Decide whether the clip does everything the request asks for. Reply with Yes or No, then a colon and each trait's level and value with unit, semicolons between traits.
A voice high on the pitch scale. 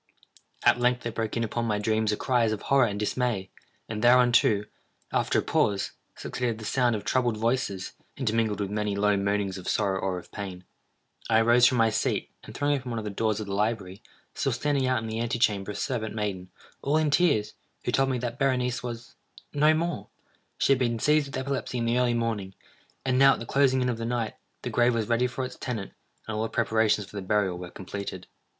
No: low, 115 Hz